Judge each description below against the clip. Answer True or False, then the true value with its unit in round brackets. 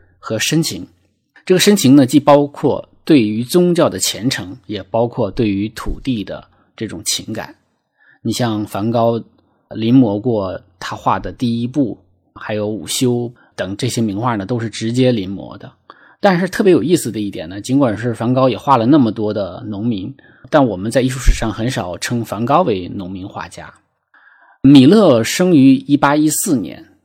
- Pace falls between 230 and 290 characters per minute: True (250 characters per minute)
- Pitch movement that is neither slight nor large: True (4.3 semitones)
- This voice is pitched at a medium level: False (120 Hz)